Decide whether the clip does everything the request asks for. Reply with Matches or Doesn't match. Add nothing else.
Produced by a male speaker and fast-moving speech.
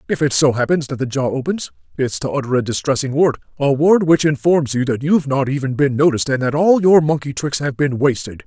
Matches